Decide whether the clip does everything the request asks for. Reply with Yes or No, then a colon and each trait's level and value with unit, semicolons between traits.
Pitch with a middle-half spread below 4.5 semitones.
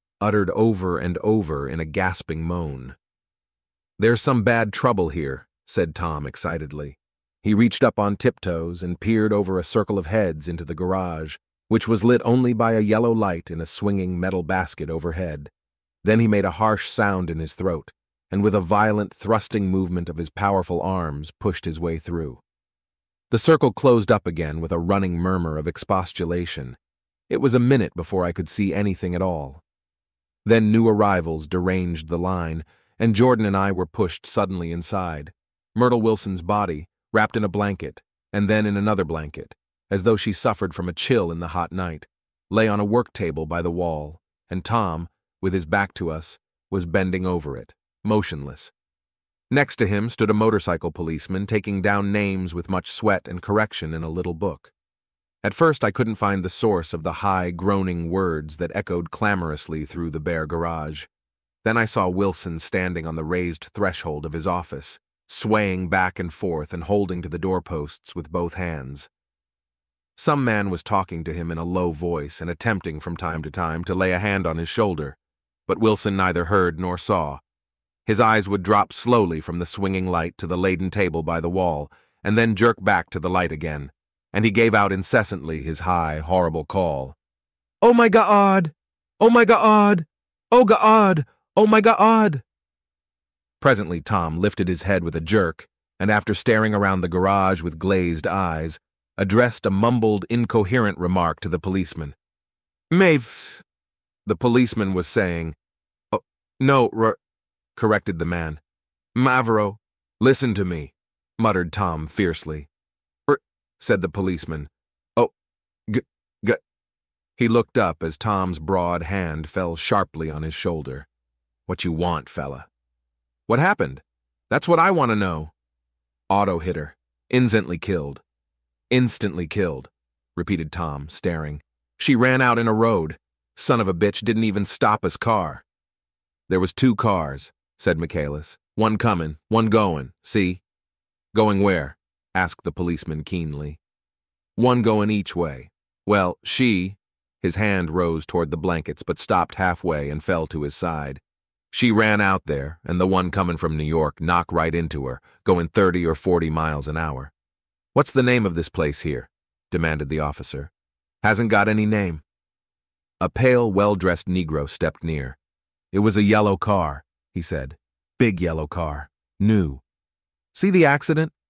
No: average, 5.2 semitones